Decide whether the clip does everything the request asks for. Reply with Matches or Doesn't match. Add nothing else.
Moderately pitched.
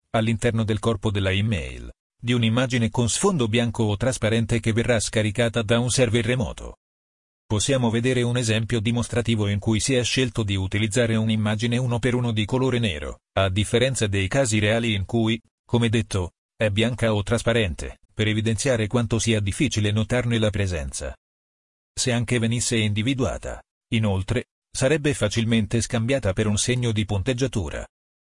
Doesn't match